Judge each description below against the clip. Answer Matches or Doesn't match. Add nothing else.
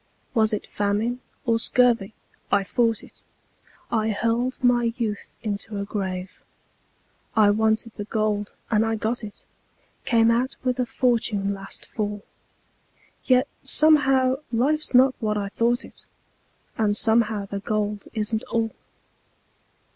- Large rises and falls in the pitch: Doesn't match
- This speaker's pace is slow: Matches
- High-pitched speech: Matches